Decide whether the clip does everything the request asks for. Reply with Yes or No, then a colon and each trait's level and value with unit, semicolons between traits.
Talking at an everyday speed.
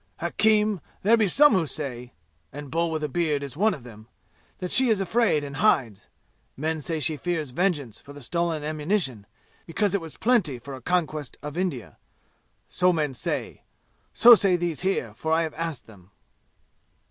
Yes: average, 180 wpm